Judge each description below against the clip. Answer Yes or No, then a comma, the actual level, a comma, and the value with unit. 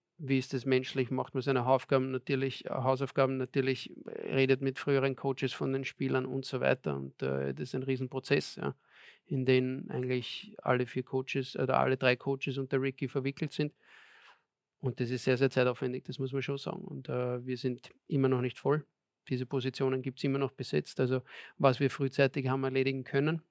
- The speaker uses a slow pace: No, fast, 190 wpm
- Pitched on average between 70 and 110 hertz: No, low, 135 Hz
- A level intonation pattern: Yes, narrow, 1.0 semitones